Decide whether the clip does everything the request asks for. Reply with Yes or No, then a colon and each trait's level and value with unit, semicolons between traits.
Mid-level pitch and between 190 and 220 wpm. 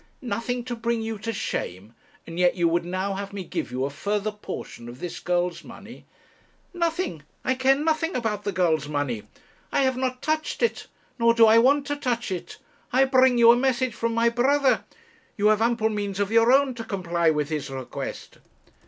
No: high, 225 Hz; average, 195 wpm